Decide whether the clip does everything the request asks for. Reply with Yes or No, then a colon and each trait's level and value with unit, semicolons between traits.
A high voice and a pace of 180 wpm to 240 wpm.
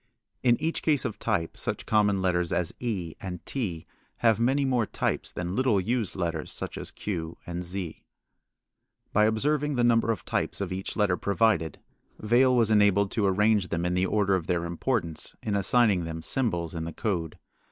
No: low, 100 Hz; average, 185 wpm